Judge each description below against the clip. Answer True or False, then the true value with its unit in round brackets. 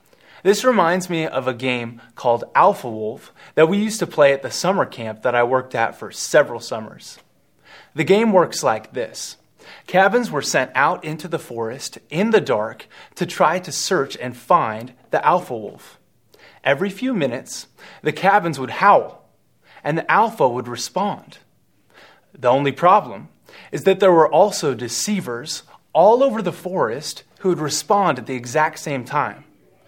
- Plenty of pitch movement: True (6.8 semitones)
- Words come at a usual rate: True (165 wpm)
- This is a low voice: False (155 Hz)